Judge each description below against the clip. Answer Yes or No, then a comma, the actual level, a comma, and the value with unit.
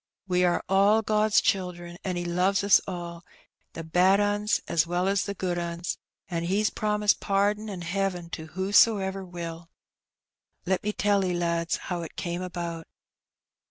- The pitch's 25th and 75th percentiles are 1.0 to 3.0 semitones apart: Yes, narrow, 2.6 semitones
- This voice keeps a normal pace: Yes, average, 160 wpm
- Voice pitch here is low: No, medium, 185 Hz